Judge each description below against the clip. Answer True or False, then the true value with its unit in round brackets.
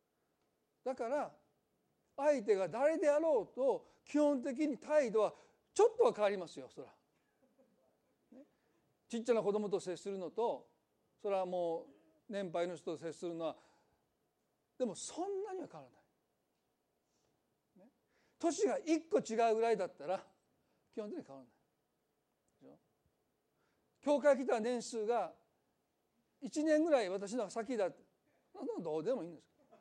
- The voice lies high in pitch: True (235 Hz)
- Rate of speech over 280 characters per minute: False (240 characters per minute)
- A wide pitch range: True (7.1 semitones)